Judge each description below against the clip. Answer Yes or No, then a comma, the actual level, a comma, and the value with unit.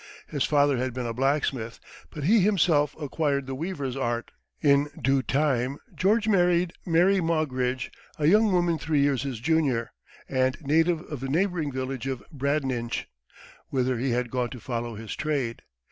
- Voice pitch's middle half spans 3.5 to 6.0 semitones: Yes, average, 4.0 semitones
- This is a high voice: No, medium, 140 Hz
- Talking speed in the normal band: Yes, average, 160 wpm